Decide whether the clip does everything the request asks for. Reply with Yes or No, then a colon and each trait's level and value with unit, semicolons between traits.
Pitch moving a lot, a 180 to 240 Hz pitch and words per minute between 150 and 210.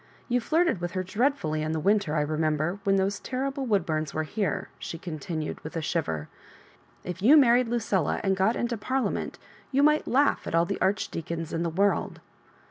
Yes: wide, 6.9 semitones; high, 190 Hz; average, 190 wpm